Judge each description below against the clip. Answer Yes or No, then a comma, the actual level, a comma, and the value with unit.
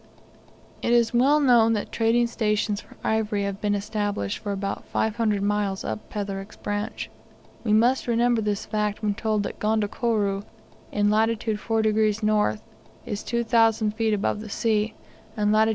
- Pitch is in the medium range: No, high, 215 Hz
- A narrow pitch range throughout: Yes, narrow, 1.6 semitones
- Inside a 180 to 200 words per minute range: No, average, 155 wpm